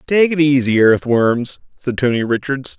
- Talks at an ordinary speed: Yes, average, 150 wpm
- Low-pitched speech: Yes, low, 130 Hz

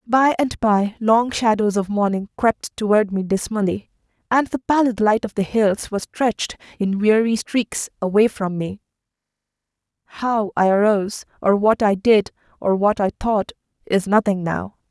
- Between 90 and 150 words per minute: No, average, 160 wpm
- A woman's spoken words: Yes, female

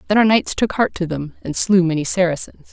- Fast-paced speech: Yes, fast, 245 wpm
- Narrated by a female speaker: Yes, female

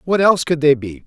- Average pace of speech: No, fast, 280 wpm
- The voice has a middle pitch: Yes, medium, 155 Hz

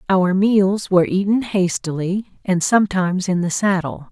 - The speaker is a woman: Yes, female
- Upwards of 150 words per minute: No, average, 145 wpm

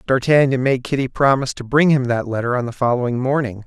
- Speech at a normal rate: No, fast, 215 wpm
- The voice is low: Yes, low, 130 Hz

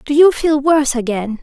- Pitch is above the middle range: Yes, very high, 275 Hz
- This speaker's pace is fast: Yes, fast, 210 wpm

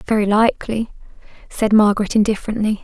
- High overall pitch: Yes, high, 215 Hz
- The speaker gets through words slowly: Yes, slow, 105 wpm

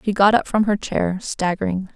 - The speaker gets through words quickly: Yes, fast, 215 wpm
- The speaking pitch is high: Yes, high, 195 Hz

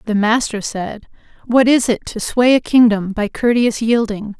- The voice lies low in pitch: No, high, 225 Hz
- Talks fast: No, average, 175 wpm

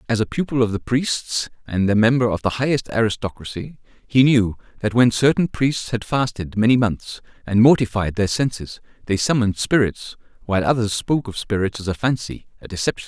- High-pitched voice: No, low, 115 Hz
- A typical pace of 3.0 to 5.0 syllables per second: No, 5.6 syllables/s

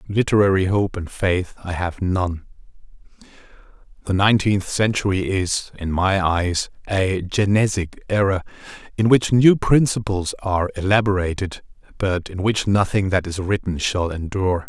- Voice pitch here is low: Yes, very low, 95 Hz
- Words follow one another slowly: Yes, slow, 130 wpm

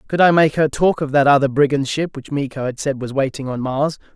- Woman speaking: No, male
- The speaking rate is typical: No, fast, 260 wpm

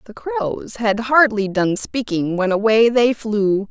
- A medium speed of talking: Yes, average, 160 wpm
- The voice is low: No, high, 225 Hz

